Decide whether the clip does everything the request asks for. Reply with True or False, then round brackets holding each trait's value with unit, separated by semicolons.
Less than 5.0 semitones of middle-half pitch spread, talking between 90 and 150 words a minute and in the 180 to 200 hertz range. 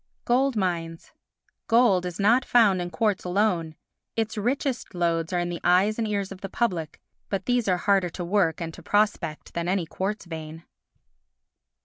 False (3.9 semitones; 170 wpm; 190 Hz)